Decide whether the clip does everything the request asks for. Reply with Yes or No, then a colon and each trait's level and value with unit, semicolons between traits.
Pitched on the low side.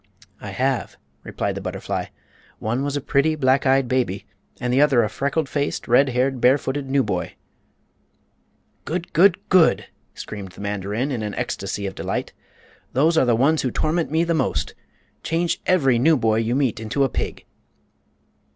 Yes: low, 130 Hz